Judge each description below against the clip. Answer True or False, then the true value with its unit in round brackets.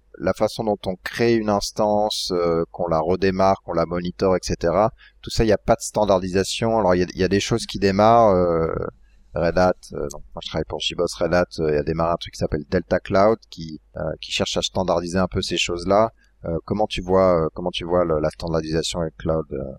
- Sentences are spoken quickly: True (235 wpm)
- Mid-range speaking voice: False (90 Hz)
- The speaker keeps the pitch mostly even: False (3.0 semitones)